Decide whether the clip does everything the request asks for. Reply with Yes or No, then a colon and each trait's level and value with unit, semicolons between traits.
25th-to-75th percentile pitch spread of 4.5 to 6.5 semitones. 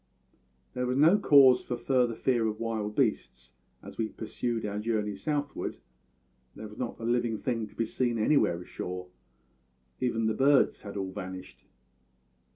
No: average, 3.1 semitones